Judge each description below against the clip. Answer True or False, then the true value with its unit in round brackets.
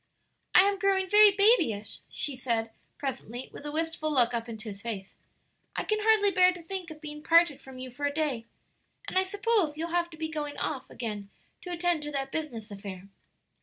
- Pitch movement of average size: False (6.9 semitones)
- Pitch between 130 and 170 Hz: False (300 Hz)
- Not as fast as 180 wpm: False (205 wpm)